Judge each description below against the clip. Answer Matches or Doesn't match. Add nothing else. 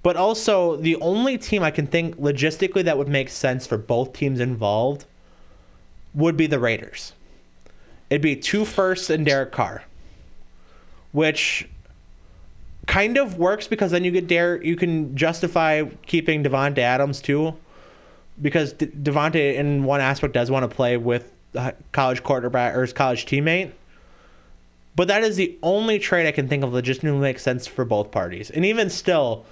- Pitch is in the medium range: Matches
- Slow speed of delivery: Doesn't match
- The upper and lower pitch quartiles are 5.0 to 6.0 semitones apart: Matches